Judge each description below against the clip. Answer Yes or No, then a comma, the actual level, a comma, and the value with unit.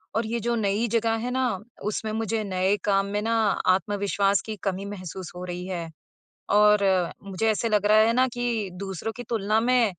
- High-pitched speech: Yes, high, 210 Hz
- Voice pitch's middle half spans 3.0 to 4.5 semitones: No, narrow, 2.5 semitones